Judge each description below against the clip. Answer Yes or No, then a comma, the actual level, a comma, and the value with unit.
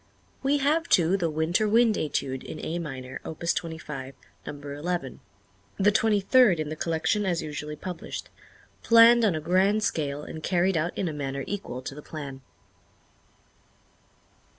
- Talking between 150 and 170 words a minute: Yes, average, 155 wpm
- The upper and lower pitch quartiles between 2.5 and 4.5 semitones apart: No, average, 5.3 semitones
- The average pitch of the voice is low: No, medium, 165 Hz